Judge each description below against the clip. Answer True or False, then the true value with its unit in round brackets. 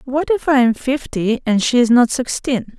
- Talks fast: True (215 wpm)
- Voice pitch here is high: True (250 Hz)